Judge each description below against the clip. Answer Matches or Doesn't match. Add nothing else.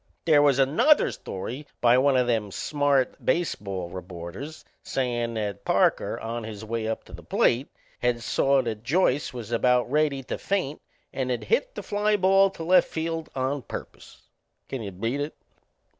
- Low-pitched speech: Matches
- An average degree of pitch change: Matches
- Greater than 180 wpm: Doesn't match